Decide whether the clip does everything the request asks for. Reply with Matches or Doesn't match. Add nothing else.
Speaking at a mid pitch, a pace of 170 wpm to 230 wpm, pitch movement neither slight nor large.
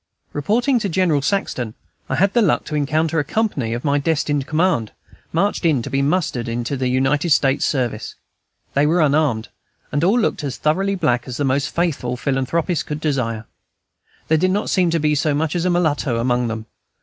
Matches